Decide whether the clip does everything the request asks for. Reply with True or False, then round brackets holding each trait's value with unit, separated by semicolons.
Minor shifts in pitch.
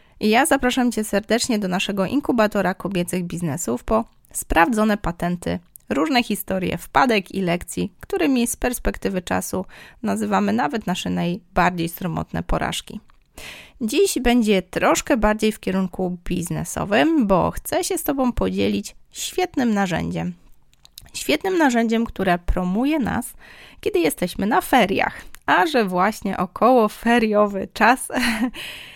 False (5.2 semitones)